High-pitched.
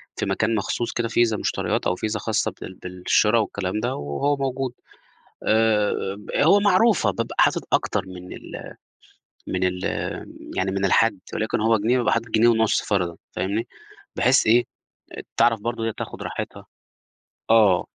No: low, 110 Hz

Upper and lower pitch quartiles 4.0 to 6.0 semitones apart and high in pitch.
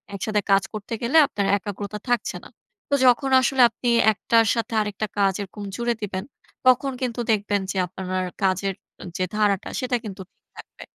No: average, 3.3 semitones; high, 210 Hz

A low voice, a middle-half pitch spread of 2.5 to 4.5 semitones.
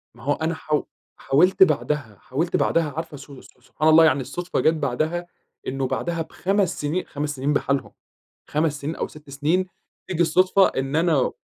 No: medium, 155 Hz; average, 3.4 semitones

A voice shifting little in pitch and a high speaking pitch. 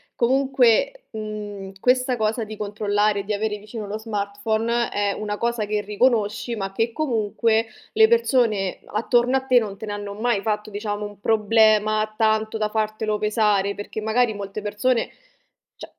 Yes: narrow, 2.0 semitones; high, 215 Hz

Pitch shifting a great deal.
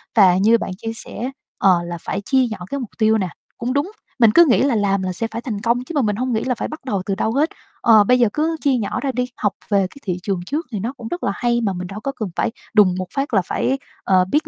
No: average, 4.6 semitones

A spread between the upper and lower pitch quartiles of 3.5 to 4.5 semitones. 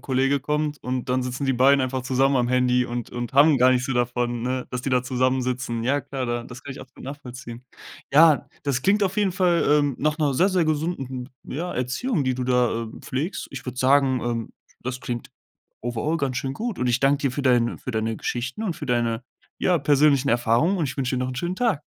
No: average, 2.8 semitones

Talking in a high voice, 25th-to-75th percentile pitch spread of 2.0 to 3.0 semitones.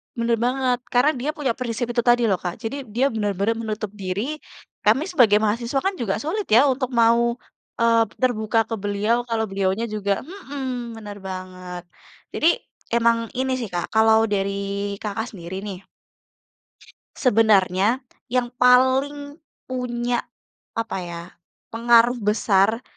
No: high, 230 Hz; average, 3.6 semitones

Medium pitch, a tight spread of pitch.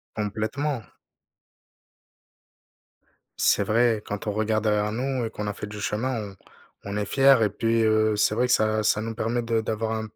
No: low, 110 Hz; narrow, 1.5 semitones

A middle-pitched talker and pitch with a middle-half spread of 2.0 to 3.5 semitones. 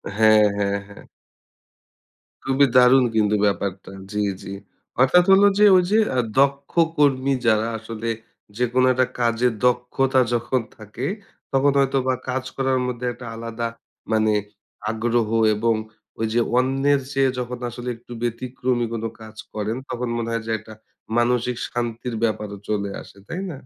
No: low, 120 Hz; average, 2.8 semitones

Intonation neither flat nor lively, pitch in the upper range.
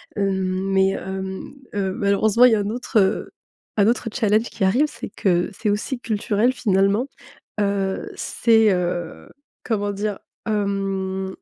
No: narrow, 2.2 semitones; high, 200 Hz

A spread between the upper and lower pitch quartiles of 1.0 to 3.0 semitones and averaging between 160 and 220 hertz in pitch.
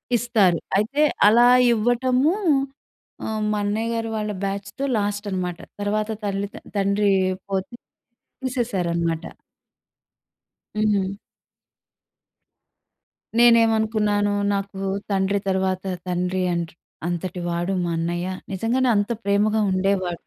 Yes: average, 2.7 semitones; high, 200 Hz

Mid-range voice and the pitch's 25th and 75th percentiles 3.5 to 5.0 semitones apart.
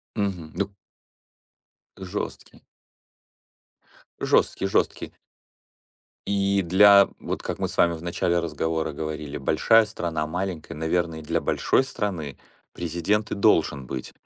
No: very low, 85 Hz; average, 3.8 semitones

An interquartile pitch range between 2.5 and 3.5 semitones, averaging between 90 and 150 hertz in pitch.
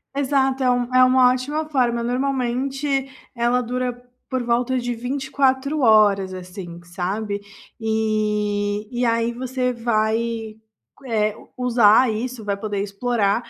No: average, 3.1 semitones; high, 240 Hz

